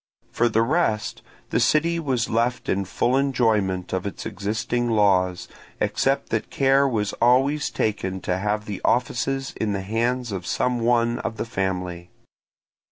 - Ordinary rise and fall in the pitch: Yes, average, 4.1 semitones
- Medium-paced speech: Yes, average, 155 wpm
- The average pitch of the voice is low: Yes, low, 115 Hz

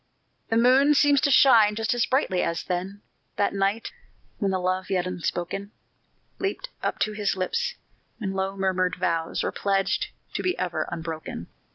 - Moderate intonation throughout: Yes, average, 4.1 semitones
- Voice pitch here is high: Yes, high, 195 Hz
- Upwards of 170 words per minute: No, average, 165 wpm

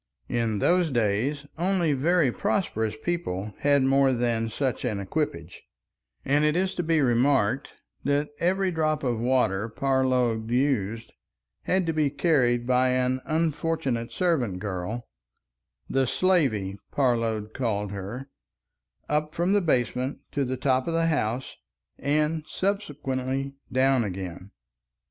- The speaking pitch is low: Yes, low, 130 Hz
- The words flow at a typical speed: No, slow, 125 wpm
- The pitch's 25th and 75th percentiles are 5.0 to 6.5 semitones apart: Yes, wide, 5.5 semitones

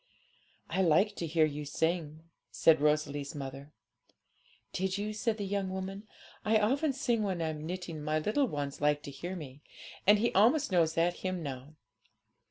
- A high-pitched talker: No, medium, 170 Hz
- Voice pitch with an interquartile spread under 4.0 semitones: No, average, 5.3 semitones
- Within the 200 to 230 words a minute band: No, average, 170 wpm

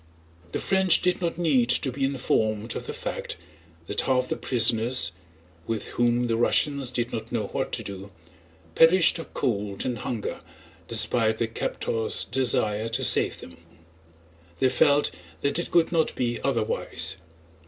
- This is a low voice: Yes, low, 120 Hz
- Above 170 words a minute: No, average, 145 wpm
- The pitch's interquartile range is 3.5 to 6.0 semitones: Yes, average, 4.2 semitones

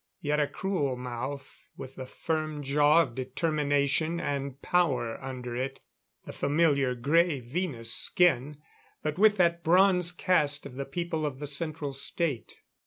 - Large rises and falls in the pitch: No, average, 3.9 semitones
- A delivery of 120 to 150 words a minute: Yes, average, 145 wpm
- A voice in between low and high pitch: Yes, medium, 145 Hz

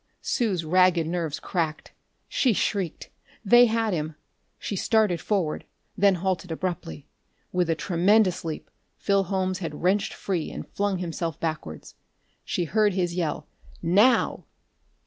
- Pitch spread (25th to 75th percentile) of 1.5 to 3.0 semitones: No, average, 3.4 semitones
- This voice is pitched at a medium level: Yes, medium, 180 Hz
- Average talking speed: No, slow, 130 wpm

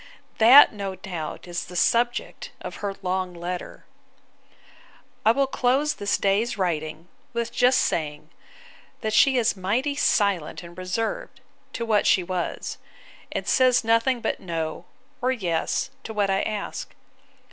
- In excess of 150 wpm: No, average, 140 wpm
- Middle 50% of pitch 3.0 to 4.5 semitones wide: No, average, 5.0 semitones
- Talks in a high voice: Yes, high, 200 Hz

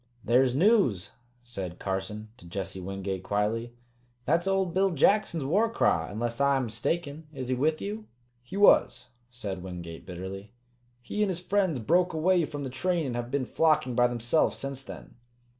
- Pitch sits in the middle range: No, low, 130 Hz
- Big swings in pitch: Yes, wide, 8.3 semitones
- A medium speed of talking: Yes, average, 170 wpm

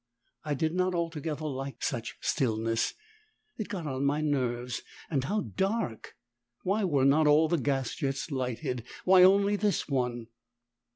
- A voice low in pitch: No, medium, 145 Hz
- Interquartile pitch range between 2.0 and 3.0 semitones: No, wide, 5.5 semitones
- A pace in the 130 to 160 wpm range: Yes, average, 150 wpm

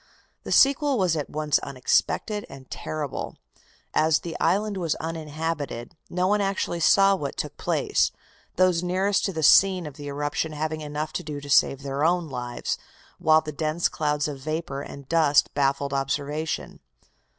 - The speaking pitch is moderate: Yes, medium, 155 Hz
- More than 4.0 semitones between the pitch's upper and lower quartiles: No, average, 3.5 semitones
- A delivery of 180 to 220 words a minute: No, average, 160 wpm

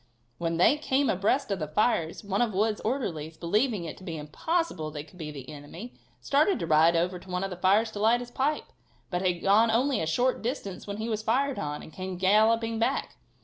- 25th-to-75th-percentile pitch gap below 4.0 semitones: No, wide, 5.6 semitones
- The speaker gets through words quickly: Yes, fast, 225 wpm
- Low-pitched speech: No, high, 200 Hz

